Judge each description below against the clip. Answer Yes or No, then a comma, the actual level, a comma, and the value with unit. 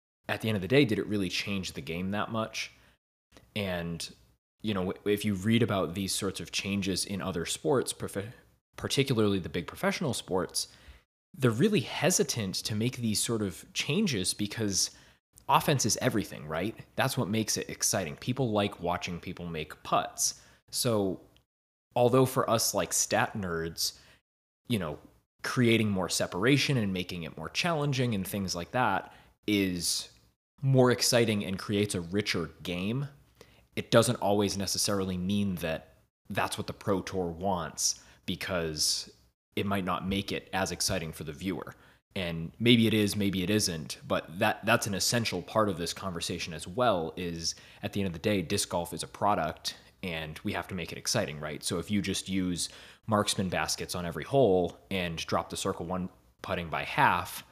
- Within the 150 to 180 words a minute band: Yes, average, 175 wpm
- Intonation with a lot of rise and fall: No, average, 3.8 semitones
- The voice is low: Yes, very low, 95 Hz